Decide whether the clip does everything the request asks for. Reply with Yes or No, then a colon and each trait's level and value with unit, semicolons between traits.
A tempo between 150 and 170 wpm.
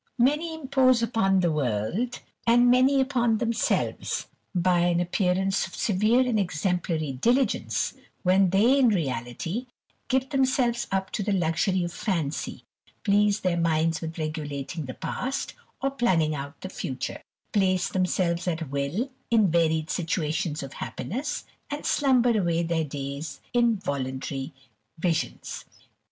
No: slow, 135 wpm